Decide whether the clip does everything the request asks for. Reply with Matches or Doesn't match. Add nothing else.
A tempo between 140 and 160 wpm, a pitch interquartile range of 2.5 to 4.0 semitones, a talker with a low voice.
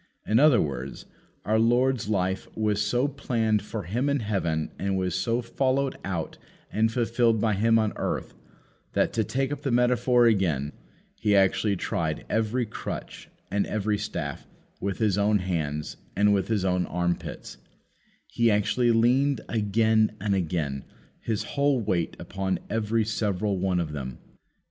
Matches